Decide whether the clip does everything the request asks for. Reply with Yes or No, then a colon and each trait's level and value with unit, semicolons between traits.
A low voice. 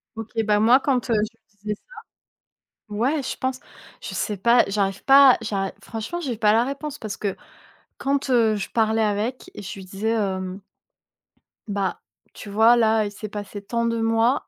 No: high, 220 Hz